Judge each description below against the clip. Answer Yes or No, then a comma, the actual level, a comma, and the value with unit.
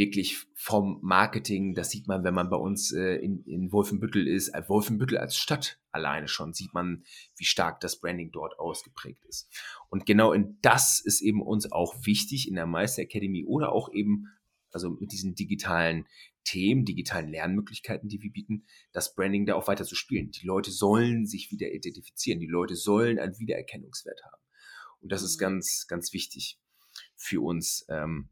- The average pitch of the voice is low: Yes, low, 100 Hz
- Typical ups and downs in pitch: No, narrow, 2.3 semitones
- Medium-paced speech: Yes, average, 180 wpm